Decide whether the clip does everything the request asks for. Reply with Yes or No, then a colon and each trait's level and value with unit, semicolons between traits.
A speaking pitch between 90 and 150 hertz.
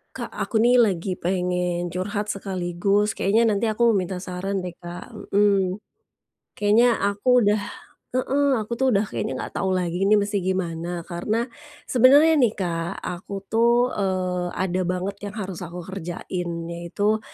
No: high, 195 Hz